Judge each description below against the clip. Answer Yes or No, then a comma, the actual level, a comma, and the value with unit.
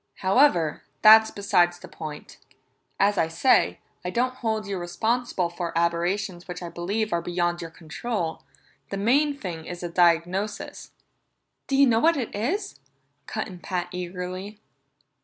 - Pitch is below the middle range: No, medium, 185 Hz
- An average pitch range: Yes, average, 4.2 semitones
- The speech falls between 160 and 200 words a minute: No, average, 150 wpm